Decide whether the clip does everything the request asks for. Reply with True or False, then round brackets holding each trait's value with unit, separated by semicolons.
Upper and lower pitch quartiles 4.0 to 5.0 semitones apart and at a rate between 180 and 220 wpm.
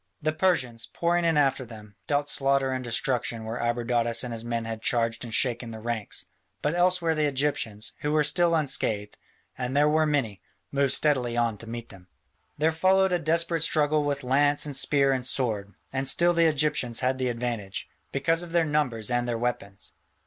True (4.5 semitones; 190 wpm)